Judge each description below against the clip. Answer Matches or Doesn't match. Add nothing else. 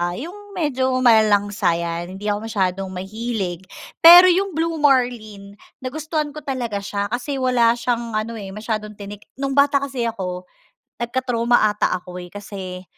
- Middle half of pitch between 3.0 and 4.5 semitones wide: Doesn't match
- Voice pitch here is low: Doesn't match